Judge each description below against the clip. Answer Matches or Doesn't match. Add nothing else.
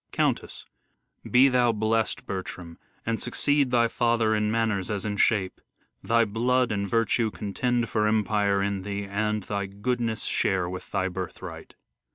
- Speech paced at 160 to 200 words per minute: Doesn't match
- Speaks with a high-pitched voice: Doesn't match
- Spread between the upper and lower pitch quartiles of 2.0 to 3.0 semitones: Matches